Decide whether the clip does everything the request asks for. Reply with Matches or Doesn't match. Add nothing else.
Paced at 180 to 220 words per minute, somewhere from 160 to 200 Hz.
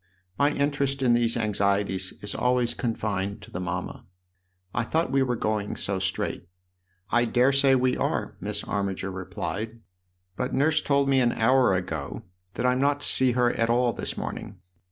Doesn't match